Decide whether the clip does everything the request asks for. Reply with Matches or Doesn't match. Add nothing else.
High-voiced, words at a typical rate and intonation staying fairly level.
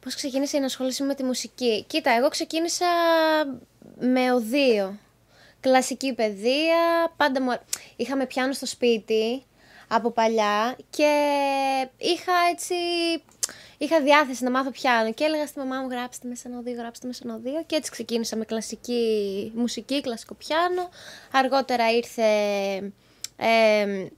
Doesn't match